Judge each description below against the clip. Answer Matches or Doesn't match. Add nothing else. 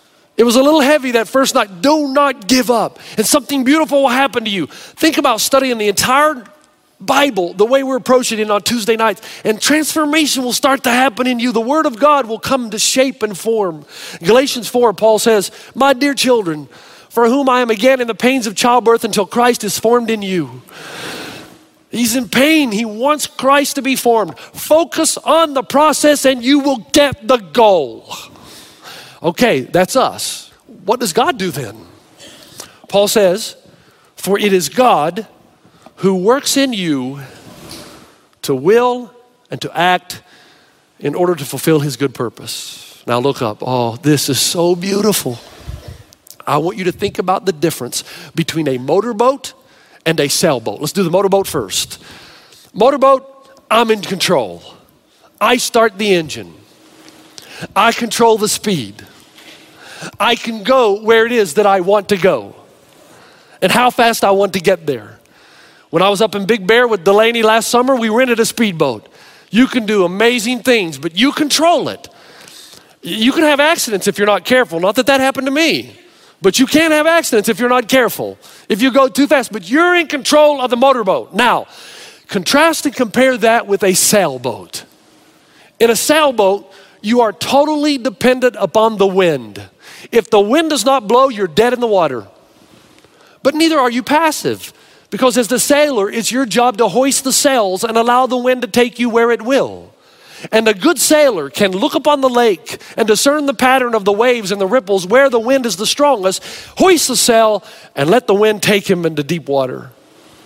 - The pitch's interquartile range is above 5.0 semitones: Matches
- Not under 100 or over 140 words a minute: Doesn't match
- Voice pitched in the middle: Doesn't match